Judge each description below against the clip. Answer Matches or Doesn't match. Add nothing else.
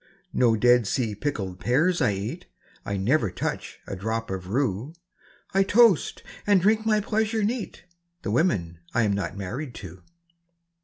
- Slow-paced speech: Doesn't match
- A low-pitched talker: Matches